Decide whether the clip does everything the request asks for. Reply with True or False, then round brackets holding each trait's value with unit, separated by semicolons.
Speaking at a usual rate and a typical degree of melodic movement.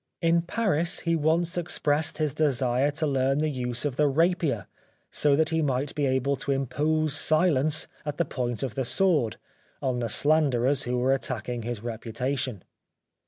True (170 wpm; 3.8 semitones)